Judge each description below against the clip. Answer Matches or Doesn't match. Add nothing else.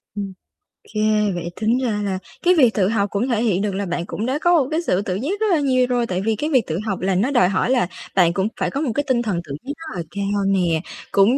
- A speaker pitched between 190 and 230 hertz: Matches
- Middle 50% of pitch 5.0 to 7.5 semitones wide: Matches